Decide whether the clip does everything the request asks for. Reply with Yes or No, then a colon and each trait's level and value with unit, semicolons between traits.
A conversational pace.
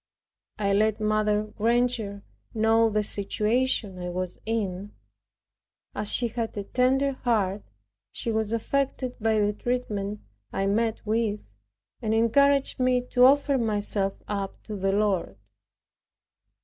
No: slow, 125 wpm